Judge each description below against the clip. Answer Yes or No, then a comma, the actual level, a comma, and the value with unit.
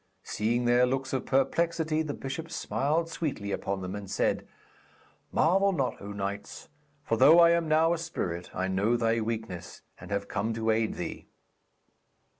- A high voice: No, low, 120 Hz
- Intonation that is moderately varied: No, wide, 7.7 semitones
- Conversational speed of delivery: Yes, average, 165 wpm